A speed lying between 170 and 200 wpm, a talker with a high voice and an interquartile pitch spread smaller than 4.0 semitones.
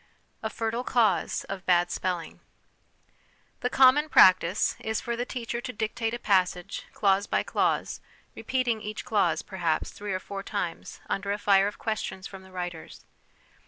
No: average, 160 wpm; high, 205 Hz; average, 3.5 semitones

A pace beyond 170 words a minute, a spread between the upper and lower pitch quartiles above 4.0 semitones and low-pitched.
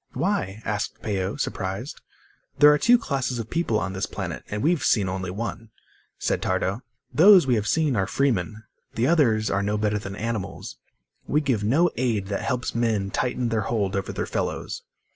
Yes: average, 180 wpm; average, 4.8 semitones; low, 110 Hz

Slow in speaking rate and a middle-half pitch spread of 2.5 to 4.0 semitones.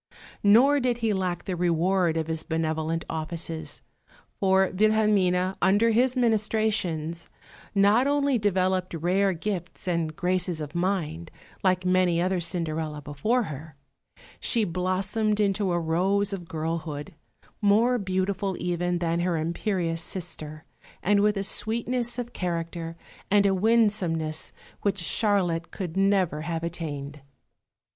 Yes: slow, 125 wpm; average, 3.7 semitones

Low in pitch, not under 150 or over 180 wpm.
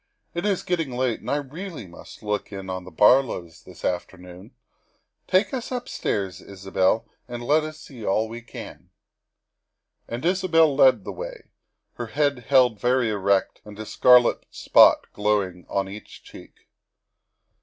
Yes: low, 120 Hz; average, 155 wpm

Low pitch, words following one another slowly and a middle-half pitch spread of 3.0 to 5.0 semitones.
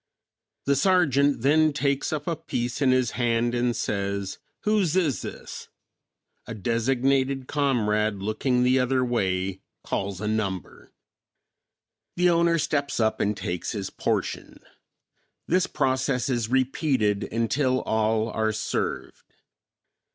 Yes: low, 125 Hz; slow, 120 wpm; average, 4.5 semitones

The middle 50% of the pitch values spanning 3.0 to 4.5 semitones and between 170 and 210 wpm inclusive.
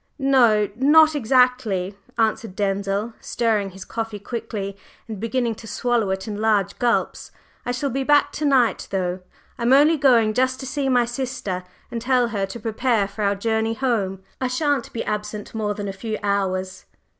Yes: average, 3.9 semitones; average, 175 wpm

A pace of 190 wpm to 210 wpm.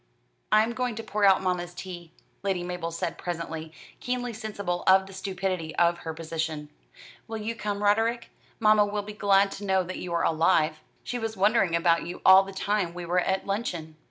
Yes: average, 195 wpm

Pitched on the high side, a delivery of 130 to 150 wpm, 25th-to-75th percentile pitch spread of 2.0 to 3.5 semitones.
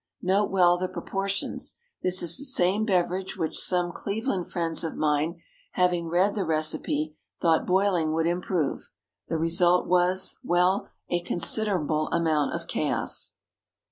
No: medium, 175 Hz; average, 140 wpm; narrow, 2.4 semitones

